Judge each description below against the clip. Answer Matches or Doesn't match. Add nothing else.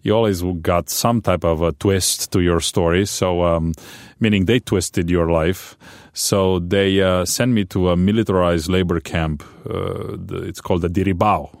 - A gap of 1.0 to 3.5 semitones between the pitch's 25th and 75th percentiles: Matches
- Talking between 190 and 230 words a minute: Doesn't match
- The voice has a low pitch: Matches